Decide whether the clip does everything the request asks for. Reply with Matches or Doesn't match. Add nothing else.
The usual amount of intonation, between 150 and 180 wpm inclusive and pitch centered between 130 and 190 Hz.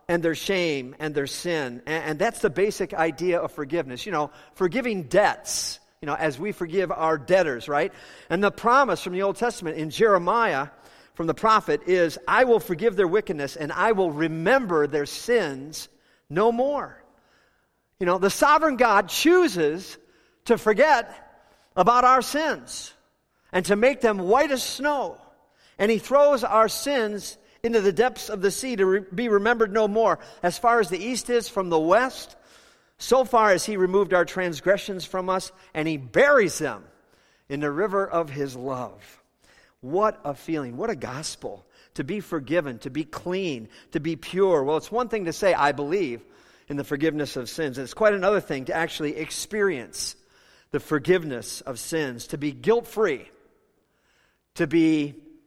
Doesn't match